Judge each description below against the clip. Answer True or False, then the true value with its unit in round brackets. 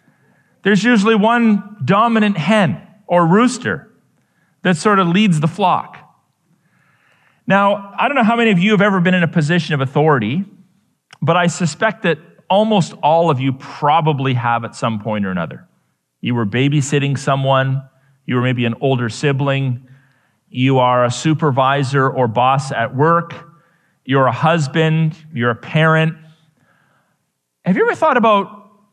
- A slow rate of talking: False (150 wpm)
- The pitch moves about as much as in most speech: False (6.5 semitones)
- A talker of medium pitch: True (160 Hz)